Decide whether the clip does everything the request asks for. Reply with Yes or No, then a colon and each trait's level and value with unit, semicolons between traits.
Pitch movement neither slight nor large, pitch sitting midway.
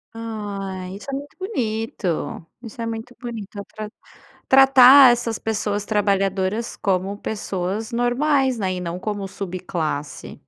No: average, 3.7 semitones; high, 210 Hz